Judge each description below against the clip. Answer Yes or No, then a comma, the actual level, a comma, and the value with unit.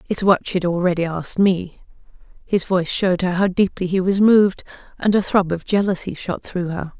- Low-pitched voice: No, medium, 185 Hz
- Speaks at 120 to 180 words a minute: No, average, 195 wpm